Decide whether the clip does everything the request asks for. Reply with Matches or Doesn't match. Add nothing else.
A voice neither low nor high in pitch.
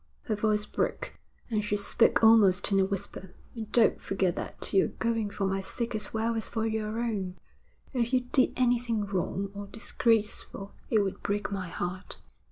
Doesn't match